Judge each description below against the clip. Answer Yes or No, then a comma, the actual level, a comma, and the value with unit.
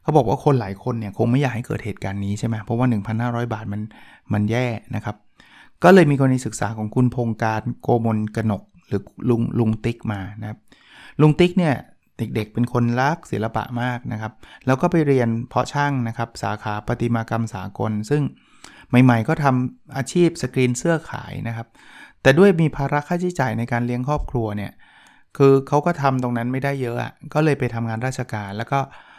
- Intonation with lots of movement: No, average, 3.8 semitones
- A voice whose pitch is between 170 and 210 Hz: No, low, 120 Hz